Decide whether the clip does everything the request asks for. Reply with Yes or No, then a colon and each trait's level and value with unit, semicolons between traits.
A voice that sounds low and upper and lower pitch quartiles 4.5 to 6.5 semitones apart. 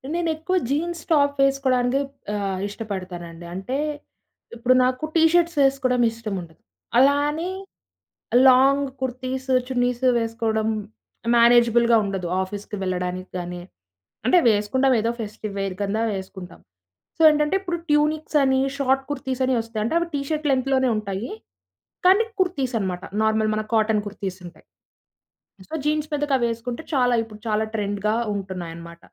No: high, 240 Hz; average, 5.1 semitones